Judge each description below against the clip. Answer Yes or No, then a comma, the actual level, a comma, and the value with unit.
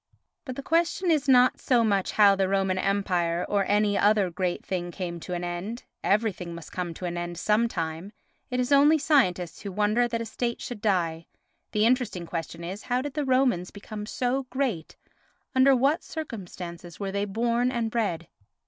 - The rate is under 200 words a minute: Yes, average, 180 wpm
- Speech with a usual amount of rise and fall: No, wide, 5.7 semitones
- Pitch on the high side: Yes, high, 205 Hz